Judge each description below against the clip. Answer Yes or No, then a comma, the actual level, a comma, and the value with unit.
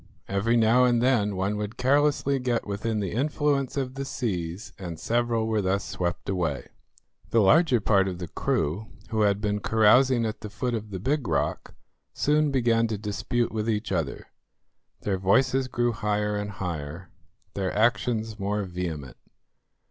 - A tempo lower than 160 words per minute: No, average, 165 wpm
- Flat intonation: No, average, 3.8 semitones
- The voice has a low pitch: Yes, low, 110 Hz